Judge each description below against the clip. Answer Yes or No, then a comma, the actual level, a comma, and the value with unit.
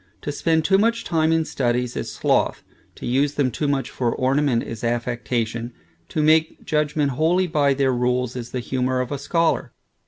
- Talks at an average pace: Yes, average, 185 wpm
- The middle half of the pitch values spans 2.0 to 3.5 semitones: No, average, 3.9 semitones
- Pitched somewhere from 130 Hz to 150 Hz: Yes, low, 135 Hz